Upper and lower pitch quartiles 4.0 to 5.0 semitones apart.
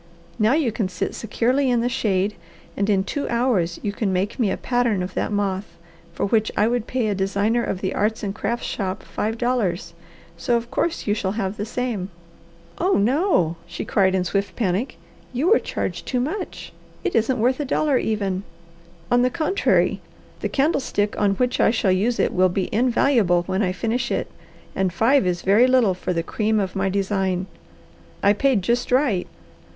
Yes: average, 4.4 semitones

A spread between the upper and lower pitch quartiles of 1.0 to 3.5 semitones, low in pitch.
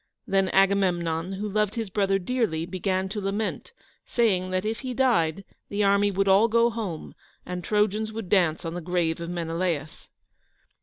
No: average, 3.1 semitones; high, 195 Hz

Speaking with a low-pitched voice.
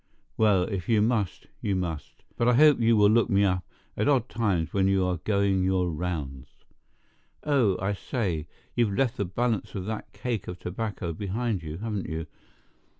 Yes: low, 100 Hz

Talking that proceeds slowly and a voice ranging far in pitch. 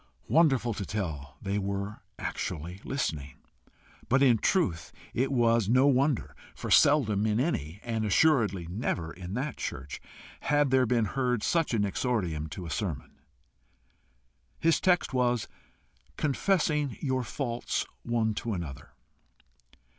Yes: slow, 130 wpm; wide, 5.9 semitones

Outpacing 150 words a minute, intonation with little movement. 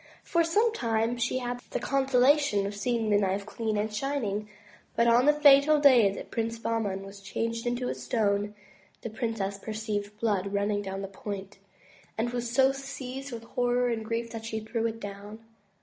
No: average, 190 wpm; average, 3.3 semitones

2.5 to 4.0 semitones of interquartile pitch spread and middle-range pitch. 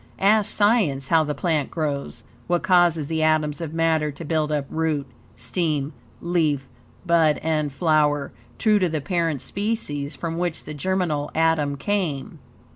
Yes: average, 2.9 semitones; medium, 160 Hz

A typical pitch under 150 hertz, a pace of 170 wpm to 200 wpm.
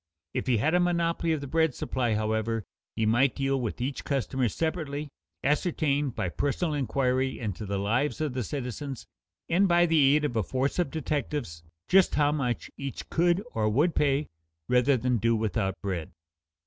Yes: low, 135 Hz; average, 175 wpm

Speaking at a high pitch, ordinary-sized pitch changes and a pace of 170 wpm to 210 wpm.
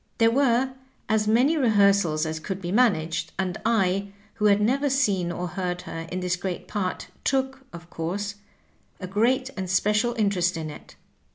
Yes: high, 200 Hz; average, 4.5 semitones; average, 175 wpm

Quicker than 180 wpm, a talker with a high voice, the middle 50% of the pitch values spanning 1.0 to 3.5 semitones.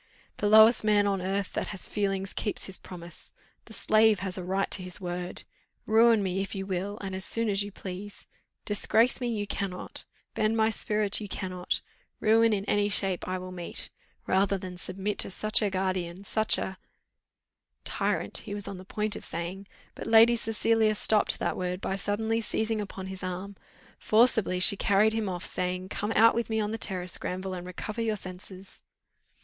Yes: average, 190 wpm; high, 200 Hz; average, 2.7 semitones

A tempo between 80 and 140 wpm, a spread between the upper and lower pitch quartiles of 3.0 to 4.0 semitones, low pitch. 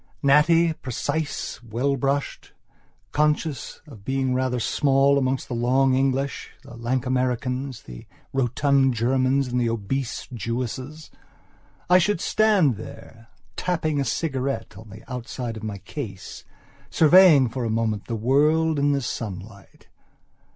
Yes: slow, 135 wpm; average, 3.4 semitones; low, 130 Hz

